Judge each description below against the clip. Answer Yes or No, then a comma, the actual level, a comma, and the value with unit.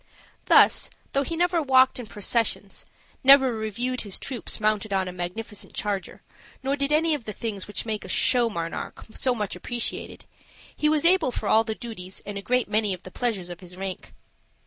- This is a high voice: Yes, high, 225 Hz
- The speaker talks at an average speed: Yes, average, 190 wpm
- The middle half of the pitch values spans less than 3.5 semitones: No, average, 4.6 semitones